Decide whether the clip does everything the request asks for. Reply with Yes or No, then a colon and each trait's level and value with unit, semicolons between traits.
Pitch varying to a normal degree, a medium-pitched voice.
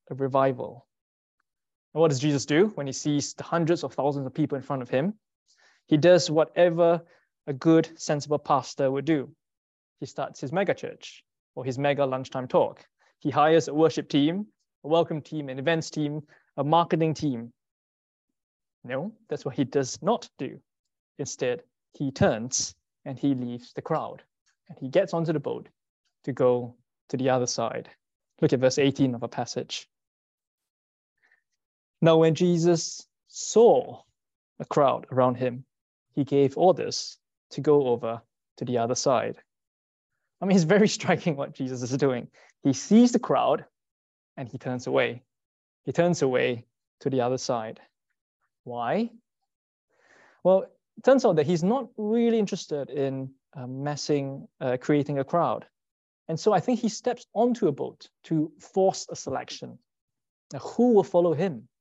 Yes: average, 4.8 semitones; medium, 145 Hz